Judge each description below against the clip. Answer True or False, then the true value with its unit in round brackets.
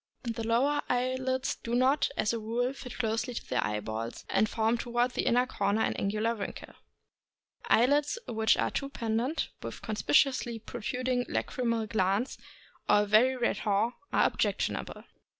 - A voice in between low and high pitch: False (235 Hz)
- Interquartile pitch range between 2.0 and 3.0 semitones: True (2.6 semitones)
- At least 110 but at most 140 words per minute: False (155 wpm)